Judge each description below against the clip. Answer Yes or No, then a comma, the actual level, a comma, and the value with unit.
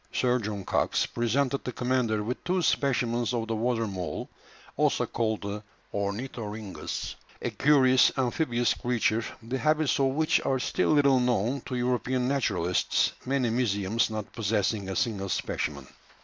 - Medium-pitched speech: No, low, 120 Hz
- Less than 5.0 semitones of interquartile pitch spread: Yes, average, 3.4 semitones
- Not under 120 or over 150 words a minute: Yes, average, 145 wpm